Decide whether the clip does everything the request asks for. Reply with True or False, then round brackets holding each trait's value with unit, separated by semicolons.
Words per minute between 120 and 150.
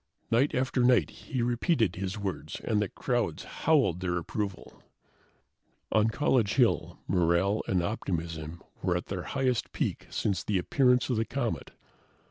True (145 wpm)